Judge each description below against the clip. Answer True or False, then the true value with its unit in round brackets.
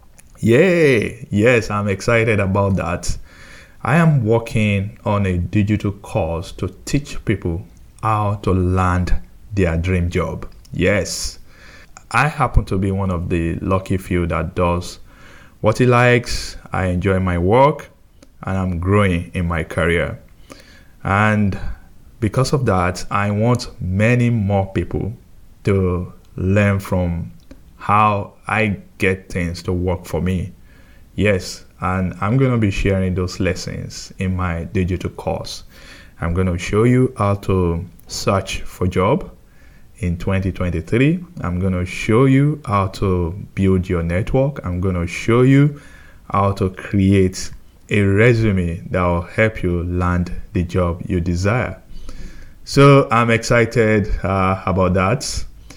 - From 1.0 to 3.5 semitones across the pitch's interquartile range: True (3.2 semitones)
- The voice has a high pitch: False (95 Hz)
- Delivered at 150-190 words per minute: False (135 wpm)